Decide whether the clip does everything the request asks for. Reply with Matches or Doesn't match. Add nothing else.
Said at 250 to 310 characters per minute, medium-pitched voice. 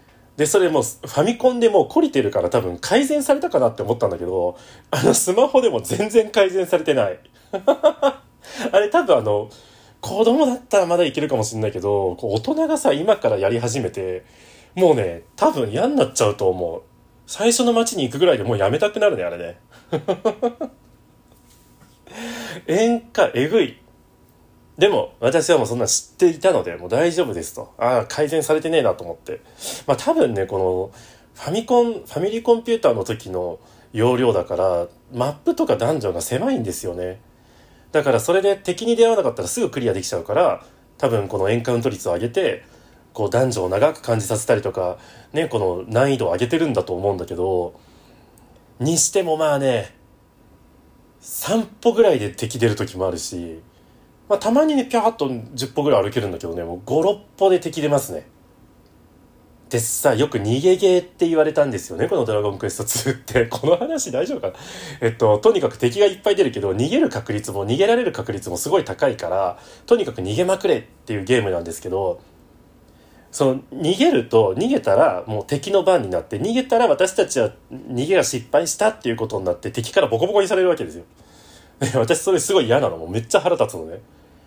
Doesn't match